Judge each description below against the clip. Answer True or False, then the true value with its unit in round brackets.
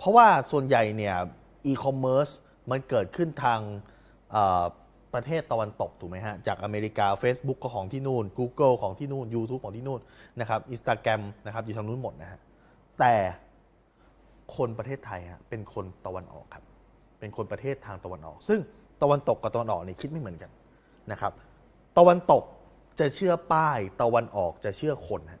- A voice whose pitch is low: True (120 Hz)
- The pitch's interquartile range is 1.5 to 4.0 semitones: False (4.8 semitones)